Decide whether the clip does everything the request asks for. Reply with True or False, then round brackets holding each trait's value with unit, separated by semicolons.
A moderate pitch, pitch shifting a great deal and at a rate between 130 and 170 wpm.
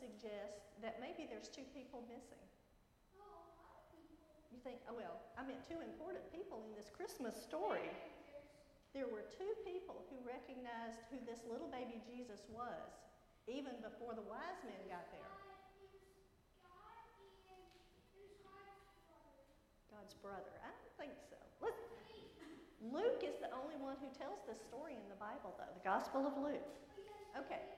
False (275 Hz; 8.6 semitones; 140 wpm)